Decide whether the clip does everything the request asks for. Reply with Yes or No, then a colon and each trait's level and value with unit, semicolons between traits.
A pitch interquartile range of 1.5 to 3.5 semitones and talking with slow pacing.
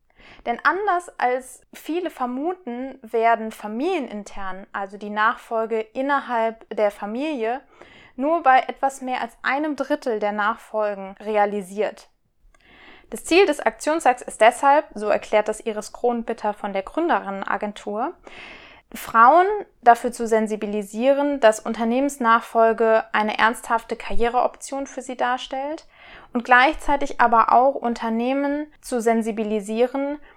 No: average, 4.1 semitones; slow, 110 wpm